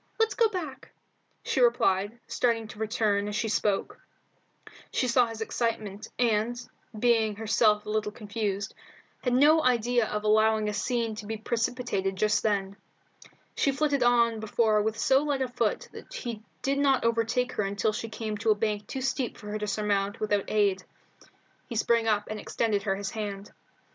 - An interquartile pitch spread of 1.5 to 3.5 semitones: Yes, narrow, 2.6 semitones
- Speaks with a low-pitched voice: No, high, 220 Hz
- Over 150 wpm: Yes, average, 175 wpm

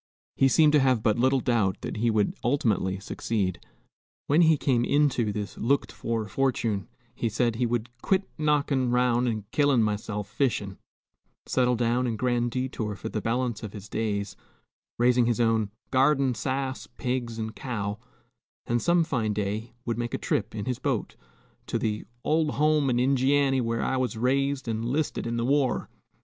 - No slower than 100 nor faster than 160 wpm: No, average, 175 wpm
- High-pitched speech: No, low, 120 Hz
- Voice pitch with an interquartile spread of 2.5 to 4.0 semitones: Yes, average, 3.3 semitones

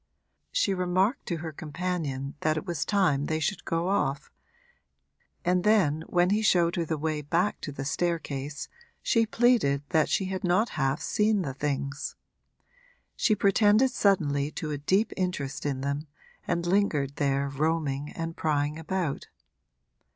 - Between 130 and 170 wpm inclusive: Yes, average, 150 wpm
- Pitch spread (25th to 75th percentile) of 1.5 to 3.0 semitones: No, average, 4.8 semitones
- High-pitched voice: No, medium, 165 Hz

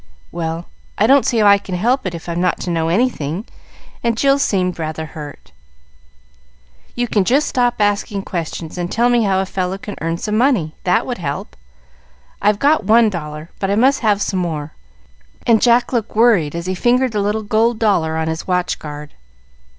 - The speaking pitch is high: Yes, high, 200 Hz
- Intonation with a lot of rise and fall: Yes, wide, 5.7 semitones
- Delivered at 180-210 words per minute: Yes, average, 190 wpm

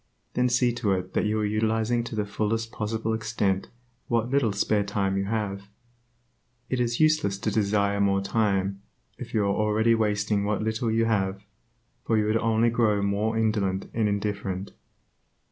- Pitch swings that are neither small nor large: No, narrow, 2.0 semitones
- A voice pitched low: Yes, low, 105 Hz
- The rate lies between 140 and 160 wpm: No, average, 170 wpm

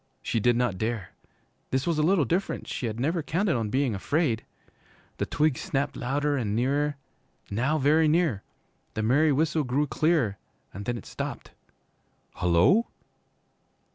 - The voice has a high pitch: No, low, 135 Hz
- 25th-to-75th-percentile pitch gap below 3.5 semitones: No, average, 5.2 semitones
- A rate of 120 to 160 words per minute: Yes, average, 150 wpm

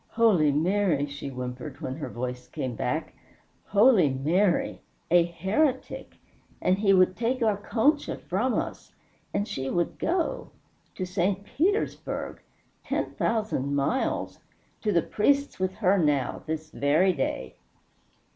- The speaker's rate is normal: No, slow, 130 wpm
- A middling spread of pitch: No, wide, 7.0 semitones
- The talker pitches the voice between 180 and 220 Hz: Yes, medium, 185 Hz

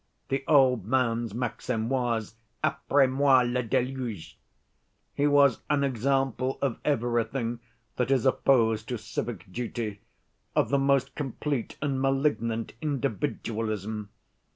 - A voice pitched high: No, low, 125 Hz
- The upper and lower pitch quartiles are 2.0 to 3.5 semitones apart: Yes, average, 3.1 semitones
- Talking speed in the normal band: No, slow, 115 wpm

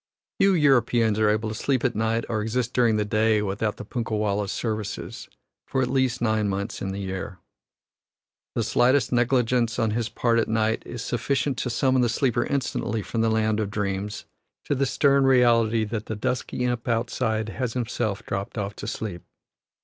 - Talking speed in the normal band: Yes, average, 185 wpm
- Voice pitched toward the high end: No, low, 115 Hz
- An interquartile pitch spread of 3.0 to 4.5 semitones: No, narrow, 2.5 semitones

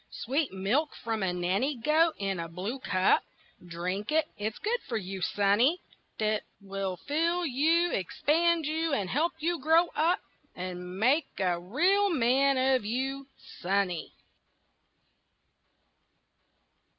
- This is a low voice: No, high, 245 Hz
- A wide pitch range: Yes, wide, 8.5 semitones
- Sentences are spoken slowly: Yes, slow, 125 wpm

